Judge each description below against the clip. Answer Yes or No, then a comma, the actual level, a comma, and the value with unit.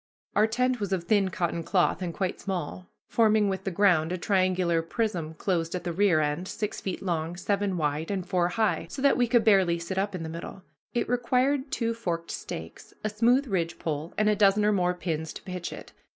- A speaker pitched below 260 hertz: Yes, high, 190 Hz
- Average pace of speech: No, fast, 210 wpm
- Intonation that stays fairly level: No, average, 3.8 semitones